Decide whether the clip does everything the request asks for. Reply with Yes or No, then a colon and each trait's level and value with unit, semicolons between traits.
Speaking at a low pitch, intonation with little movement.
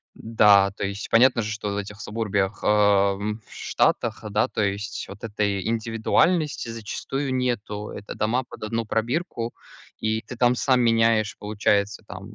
Yes: low, 110 Hz; narrow, 2.2 semitones